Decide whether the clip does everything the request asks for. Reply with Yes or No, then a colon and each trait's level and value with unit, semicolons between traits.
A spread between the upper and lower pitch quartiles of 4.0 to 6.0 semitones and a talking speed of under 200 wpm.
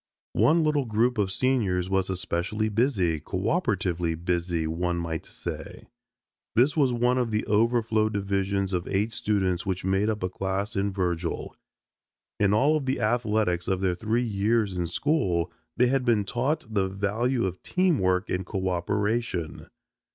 Yes: average, 4.3 semitones; average, 155 wpm